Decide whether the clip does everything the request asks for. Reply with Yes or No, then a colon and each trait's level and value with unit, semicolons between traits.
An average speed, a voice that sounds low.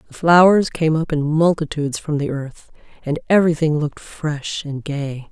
No: average, 170 wpm; medium, 155 Hz